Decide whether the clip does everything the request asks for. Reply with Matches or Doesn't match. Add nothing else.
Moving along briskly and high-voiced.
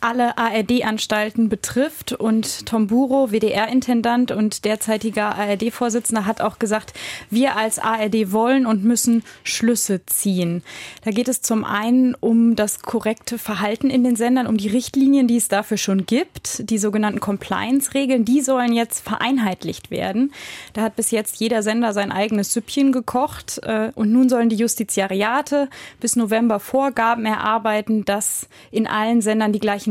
Doesn't match